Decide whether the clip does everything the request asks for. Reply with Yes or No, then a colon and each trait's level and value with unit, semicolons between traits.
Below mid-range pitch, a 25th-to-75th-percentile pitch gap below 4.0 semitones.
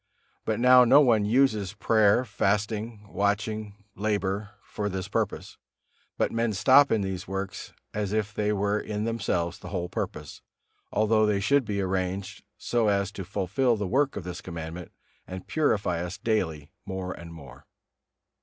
Yes: low, 105 Hz; narrow, 2.5 semitones